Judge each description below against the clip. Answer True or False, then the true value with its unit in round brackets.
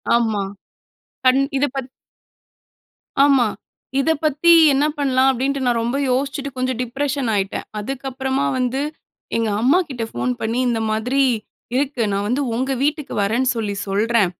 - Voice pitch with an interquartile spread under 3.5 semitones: True (2.9 semitones)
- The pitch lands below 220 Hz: False (255 Hz)